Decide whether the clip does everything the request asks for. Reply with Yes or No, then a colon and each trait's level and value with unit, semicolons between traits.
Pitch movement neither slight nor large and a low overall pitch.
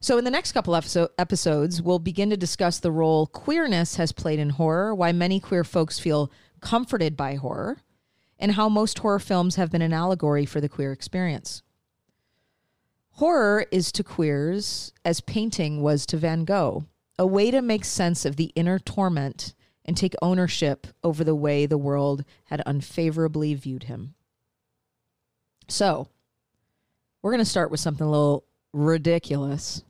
No: average, 4.0 semitones; medium, 170 Hz